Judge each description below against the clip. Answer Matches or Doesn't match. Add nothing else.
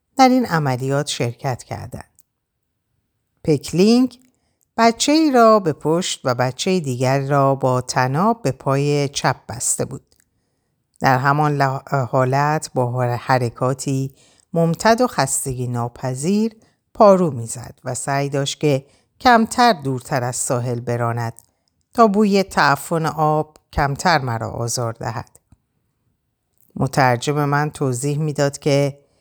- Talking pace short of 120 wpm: Matches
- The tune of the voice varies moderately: Matches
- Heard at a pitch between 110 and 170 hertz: Matches